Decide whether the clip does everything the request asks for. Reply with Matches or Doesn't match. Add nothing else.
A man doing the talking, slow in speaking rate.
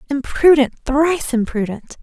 Doesn't match